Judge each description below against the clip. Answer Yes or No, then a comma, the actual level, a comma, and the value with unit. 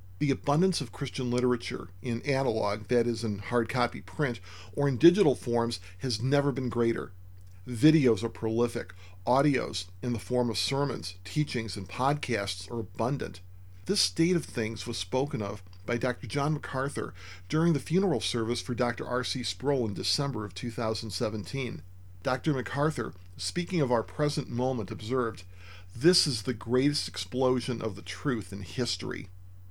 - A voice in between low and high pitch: No, low, 120 Hz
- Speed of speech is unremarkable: Yes, average, 155 wpm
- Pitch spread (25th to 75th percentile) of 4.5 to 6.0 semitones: Yes, wide, 5.5 semitones